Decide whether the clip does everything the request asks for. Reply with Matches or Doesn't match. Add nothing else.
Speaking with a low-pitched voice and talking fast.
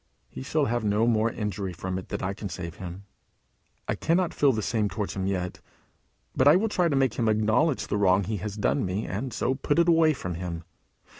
Matches